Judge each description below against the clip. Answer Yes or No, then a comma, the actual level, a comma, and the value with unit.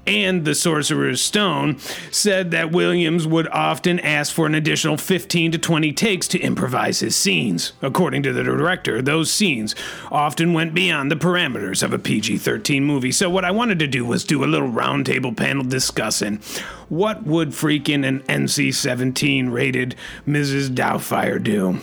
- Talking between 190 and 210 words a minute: No, average, 160 wpm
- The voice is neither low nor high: Yes, medium, 155 Hz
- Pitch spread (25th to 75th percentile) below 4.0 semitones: No, average, 4.4 semitones